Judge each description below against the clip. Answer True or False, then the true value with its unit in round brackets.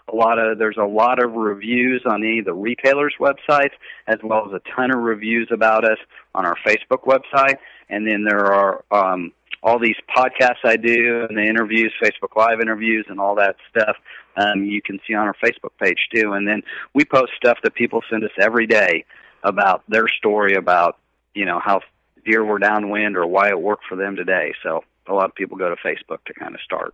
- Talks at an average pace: False (215 wpm)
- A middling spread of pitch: False (2.3 semitones)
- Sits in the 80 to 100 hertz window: False (110 Hz)